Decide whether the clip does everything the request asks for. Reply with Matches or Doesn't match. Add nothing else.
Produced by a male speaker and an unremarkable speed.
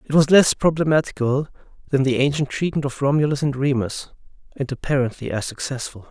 Matches